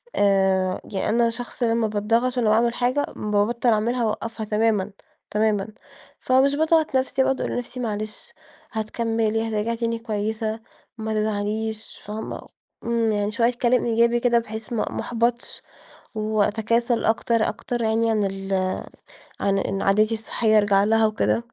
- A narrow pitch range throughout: Yes, narrow, 1.9 semitones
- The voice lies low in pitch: No, high, 220 Hz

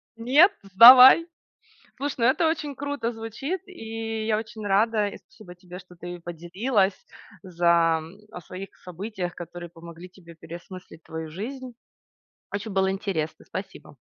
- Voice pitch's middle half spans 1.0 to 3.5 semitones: No, average, 4.7 semitones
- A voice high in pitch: Yes, high, 195 Hz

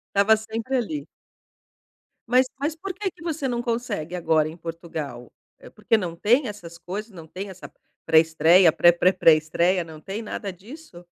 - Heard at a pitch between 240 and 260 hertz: No, medium, 185 Hz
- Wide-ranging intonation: Yes, wide, 5.8 semitones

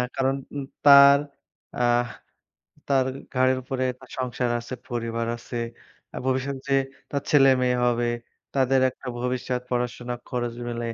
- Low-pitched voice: Yes, low, 125 Hz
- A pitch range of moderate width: No, narrow, 1.6 semitones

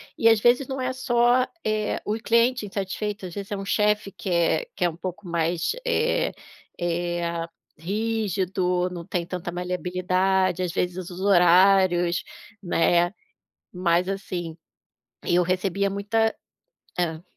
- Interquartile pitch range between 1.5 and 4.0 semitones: Yes, average, 3.0 semitones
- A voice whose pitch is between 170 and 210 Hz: Yes, medium, 185 Hz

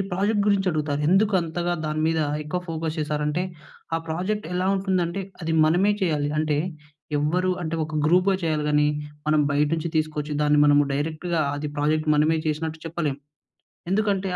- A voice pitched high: No, medium, 160 Hz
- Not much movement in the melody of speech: No, average, 3.2 semitones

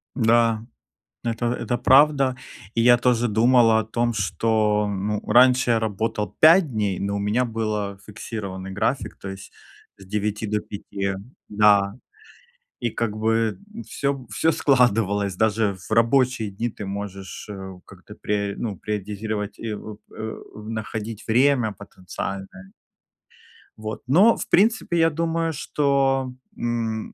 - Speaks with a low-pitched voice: Yes, low, 110 Hz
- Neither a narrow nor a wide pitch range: Yes, average, 3.2 semitones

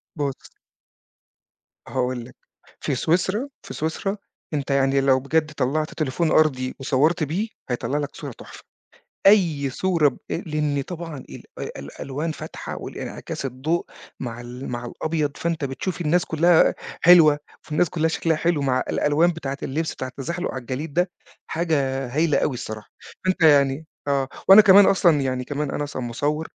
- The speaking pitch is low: No, medium, 150 Hz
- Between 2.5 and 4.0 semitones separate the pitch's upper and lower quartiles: Yes, average, 3.6 semitones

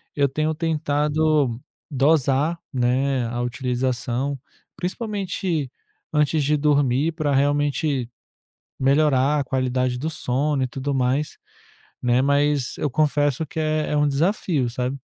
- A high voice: No, medium, 145 Hz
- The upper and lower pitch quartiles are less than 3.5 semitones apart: Yes, average, 2.8 semitones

